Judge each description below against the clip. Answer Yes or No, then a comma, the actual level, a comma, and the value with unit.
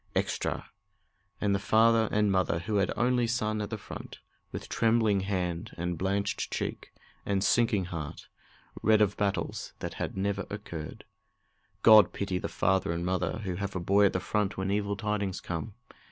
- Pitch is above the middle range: No, low, 100 Hz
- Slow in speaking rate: No, average, 175 wpm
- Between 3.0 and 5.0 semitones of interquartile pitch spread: No, narrow, 2.4 semitones